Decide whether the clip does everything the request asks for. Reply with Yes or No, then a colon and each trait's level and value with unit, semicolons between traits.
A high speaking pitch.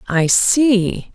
Yes: high, 215 Hz